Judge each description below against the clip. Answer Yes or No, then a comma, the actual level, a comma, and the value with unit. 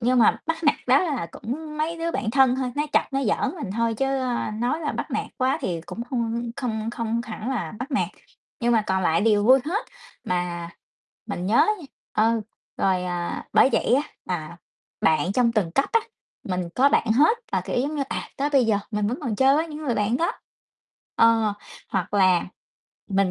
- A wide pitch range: No, average, 5.0 semitones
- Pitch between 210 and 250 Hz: Yes, high, 235 Hz